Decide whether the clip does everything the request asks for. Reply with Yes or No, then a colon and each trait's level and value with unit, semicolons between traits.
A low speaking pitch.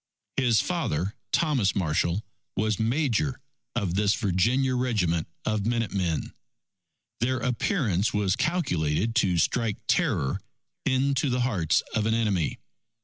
Yes: low, 110 Hz